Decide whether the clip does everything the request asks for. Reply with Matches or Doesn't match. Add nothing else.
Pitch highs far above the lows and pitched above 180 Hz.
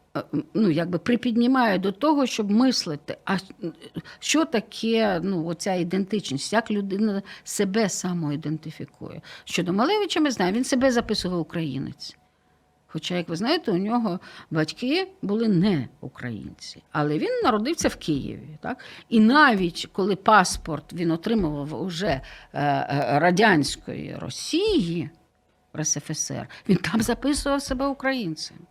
Matches